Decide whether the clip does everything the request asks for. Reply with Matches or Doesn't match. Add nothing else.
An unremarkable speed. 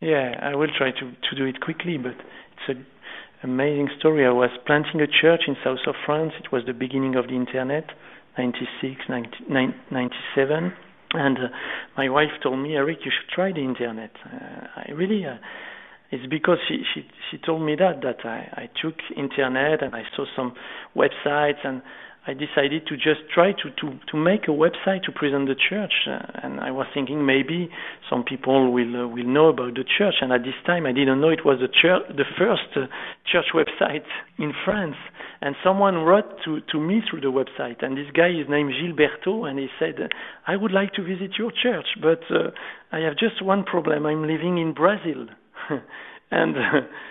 Matches